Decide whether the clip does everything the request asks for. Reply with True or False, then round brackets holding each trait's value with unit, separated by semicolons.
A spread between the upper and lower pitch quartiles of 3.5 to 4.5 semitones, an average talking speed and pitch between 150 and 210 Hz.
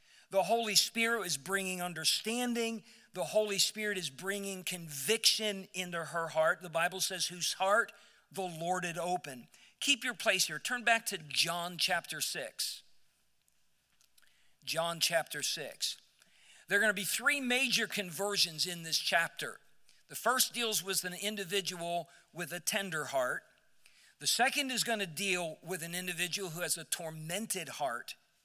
True (3.8 semitones; 150 wpm; 185 Hz)